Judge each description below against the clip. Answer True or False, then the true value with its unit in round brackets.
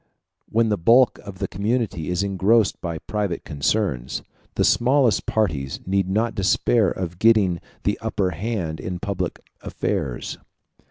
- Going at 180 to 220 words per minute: False (140 wpm)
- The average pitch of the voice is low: True (100 Hz)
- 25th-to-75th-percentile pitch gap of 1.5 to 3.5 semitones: False (4.3 semitones)